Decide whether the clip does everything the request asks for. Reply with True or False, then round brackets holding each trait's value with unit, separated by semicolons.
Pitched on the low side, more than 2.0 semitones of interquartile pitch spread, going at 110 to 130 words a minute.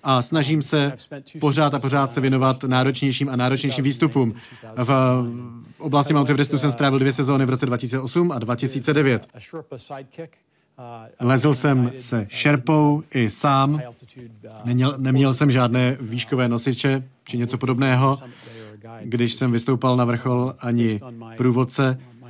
True (130 Hz; 2.4 semitones; 125 wpm)